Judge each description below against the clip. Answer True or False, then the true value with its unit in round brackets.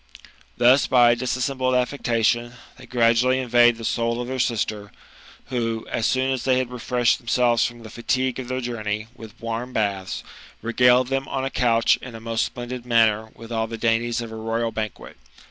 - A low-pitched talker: True (120 Hz)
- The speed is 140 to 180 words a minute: False (190 wpm)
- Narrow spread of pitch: True (1.7 semitones)